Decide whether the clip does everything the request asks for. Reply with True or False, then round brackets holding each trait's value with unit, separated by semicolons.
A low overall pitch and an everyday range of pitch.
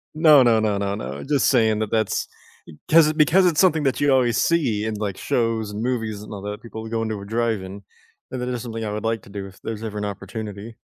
True (110 Hz; 3.3 semitones)